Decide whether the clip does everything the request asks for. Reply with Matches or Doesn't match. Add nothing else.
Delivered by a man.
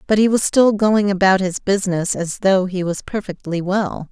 Doesn't match